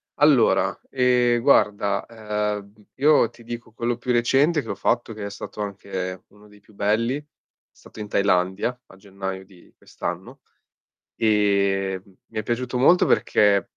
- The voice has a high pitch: No, low, 105 Hz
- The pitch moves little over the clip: No, average, 3.2 semitones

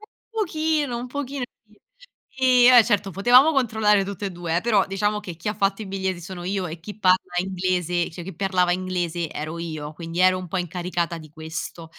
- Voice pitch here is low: No, medium, 185 Hz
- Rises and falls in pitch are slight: No, average, 3.4 semitones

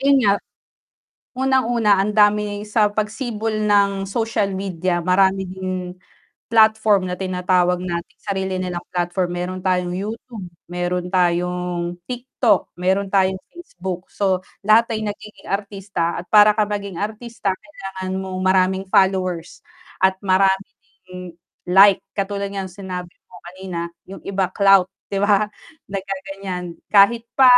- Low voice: No, high, 195 Hz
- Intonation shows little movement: Yes, narrow, 2.3 semitones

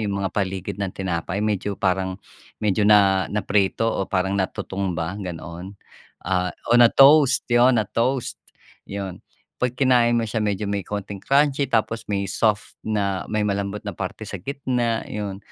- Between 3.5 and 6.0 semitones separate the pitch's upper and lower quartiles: No, average, 3.0 semitones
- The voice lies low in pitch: Yes, low, 100 Hz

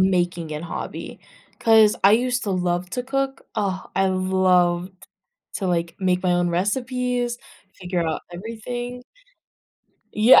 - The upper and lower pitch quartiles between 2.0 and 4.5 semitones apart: No, average, 5.1 semitones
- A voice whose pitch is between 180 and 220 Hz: Yes, high, 190 Hz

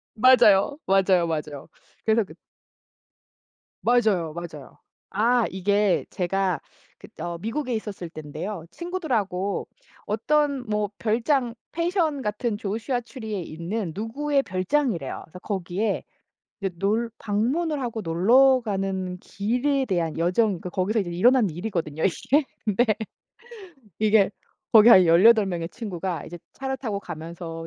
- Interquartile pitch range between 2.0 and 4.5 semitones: No, average, 5.1 semitones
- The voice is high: Yes, high, 210 Hz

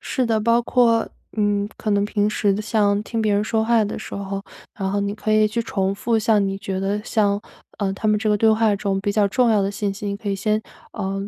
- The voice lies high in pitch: Yes, high, 210 Hz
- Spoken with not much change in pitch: Yes, narrow, 1.5 semitones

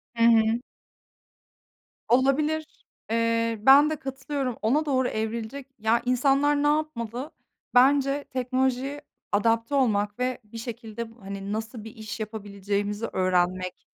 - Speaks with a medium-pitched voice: No, high, 235 Hz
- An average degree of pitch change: Yes, average, 3.7 semitones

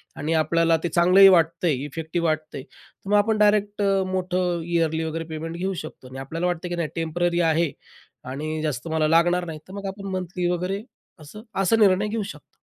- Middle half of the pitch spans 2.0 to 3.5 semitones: Yes, average, 3.1 semitones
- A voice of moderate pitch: Yes, medium, 170 Hz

